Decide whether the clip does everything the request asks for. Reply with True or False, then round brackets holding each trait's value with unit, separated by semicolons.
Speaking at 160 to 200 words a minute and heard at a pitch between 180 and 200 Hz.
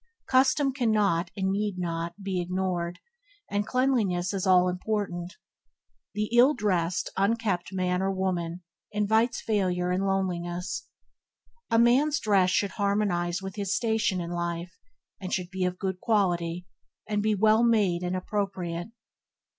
False (140 wpm; 190 Hz)